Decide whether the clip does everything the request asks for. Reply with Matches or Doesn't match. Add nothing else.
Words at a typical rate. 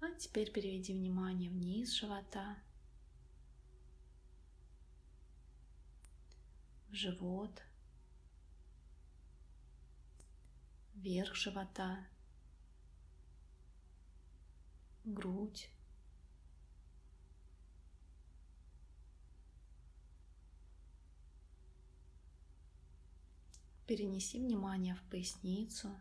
Doesn't match